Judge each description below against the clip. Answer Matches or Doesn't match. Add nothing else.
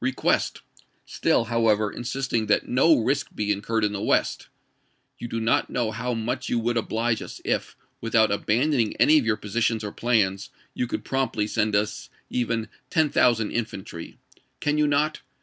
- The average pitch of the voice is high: Doesn't match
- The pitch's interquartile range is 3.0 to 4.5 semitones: Doesn't match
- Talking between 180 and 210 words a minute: Doesn't match